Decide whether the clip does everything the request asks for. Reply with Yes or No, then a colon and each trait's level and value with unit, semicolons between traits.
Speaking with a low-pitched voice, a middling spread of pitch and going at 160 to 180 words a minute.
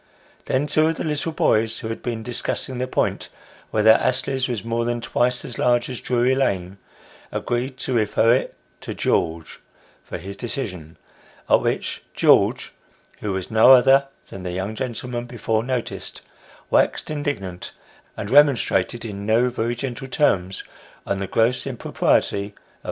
Yes: low, 120 Hz; average, 3.9 semitones; average, 165 wpm